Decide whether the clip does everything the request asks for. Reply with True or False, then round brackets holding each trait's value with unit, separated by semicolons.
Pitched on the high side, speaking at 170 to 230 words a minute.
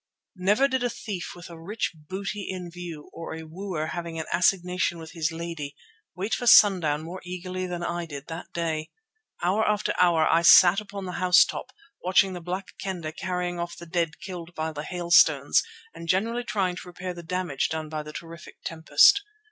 False (175 Hz; 190 wpm)